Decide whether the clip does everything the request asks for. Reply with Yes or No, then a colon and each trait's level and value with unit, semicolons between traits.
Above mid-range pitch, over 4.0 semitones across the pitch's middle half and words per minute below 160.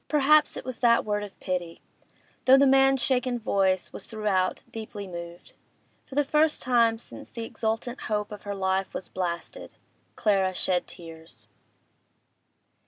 Yes: high, 210 Hz; average, 5.0 semitones; average, 145 wpm